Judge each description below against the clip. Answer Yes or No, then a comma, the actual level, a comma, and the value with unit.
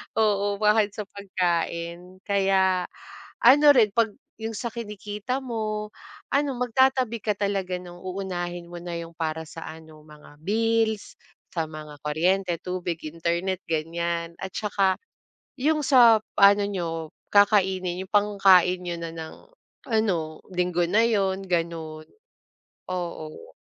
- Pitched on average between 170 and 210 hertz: Yes, high, 190 Hz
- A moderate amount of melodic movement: Yes, average, 3.7 semitones